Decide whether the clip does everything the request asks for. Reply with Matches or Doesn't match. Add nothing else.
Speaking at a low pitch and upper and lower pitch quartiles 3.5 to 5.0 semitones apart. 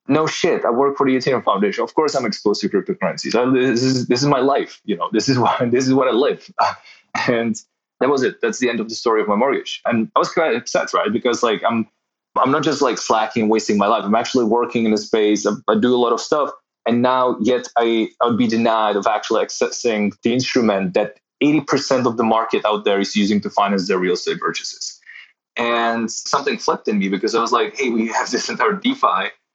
Doesn't match